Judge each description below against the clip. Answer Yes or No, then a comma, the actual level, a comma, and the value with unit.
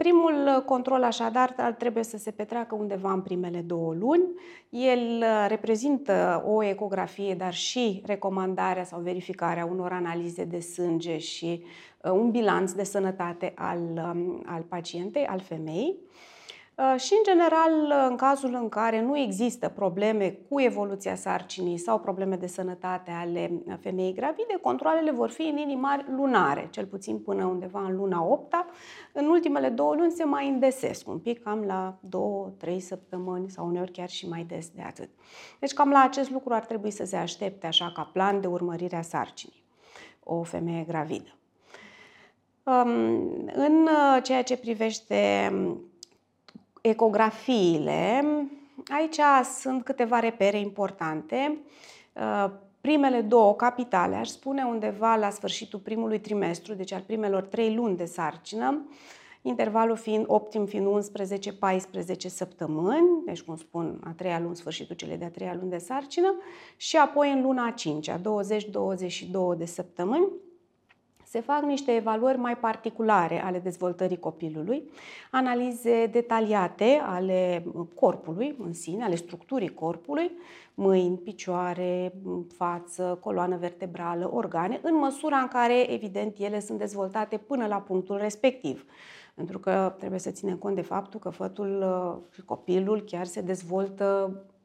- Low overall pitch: No, high, 200 Hz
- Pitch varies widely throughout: Yes, wide, 5.9 semitones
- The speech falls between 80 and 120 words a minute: No, average, 140 wpm